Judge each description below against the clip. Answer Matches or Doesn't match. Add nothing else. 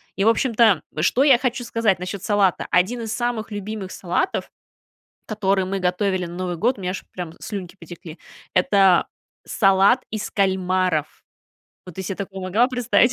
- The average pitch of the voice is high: Matches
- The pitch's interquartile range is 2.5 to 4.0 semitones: Matches